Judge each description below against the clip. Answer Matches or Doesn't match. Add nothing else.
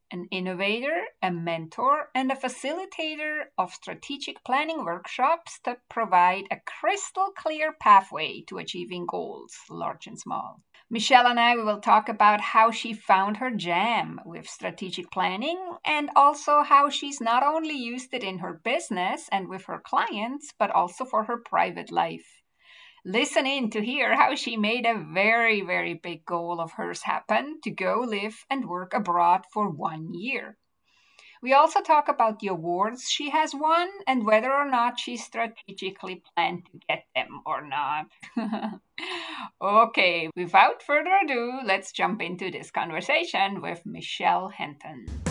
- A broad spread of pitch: Matches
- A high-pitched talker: Matches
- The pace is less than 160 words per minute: Matches